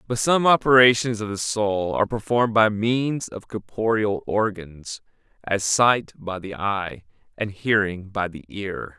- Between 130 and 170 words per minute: Yes, average, 155 wpm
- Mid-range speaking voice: No, low, 105 Hz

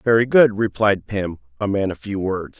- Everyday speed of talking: No, fast, 210 wpm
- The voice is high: No, low, 105 Hz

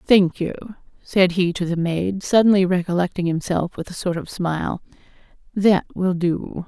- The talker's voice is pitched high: No, medium, 180 Hz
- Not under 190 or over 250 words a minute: No, average, 160 wpm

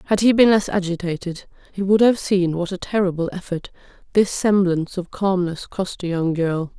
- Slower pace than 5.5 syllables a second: Yes, 5.1 syllables/s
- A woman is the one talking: Yes, female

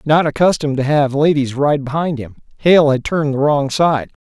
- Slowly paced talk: No, average, 200 wpm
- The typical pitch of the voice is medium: Yes, medium, 145 Hz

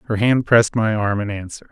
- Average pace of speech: No, fast, 245 wpm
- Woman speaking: No, male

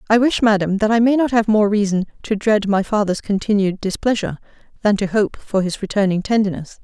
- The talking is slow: No, average, 200 wpm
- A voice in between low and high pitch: No, high, 205 Hz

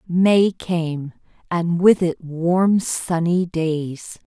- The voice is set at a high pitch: No, medium, 170 Hz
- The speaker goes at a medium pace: No, slow, 110 wpm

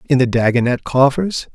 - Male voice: Yes, male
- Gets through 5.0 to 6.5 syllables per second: Yes, 5.6 syllables/s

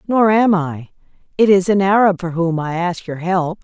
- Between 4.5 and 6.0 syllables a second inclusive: Yes, 4.7 syllables/s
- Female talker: Yes, female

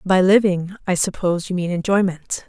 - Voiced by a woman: Yes, female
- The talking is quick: No, average, 170 wpm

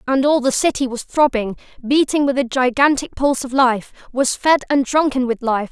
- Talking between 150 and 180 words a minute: No, average, 190 wpm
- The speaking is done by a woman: Yes, female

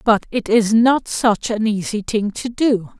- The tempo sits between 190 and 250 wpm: Yes, average, 200 wpm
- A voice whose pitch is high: Yes, high, 215 Hz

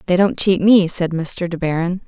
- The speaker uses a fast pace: Yes, fast, 230 wpm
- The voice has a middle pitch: Yes, medium, 180 Hz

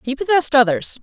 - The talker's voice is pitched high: Yes, very high, 275 Hz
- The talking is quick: No, average, 175 wpm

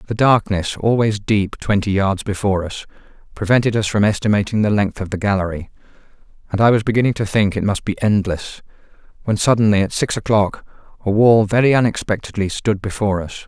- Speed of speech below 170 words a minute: No, average, 175 wpm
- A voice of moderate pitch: No, low, 105 Hz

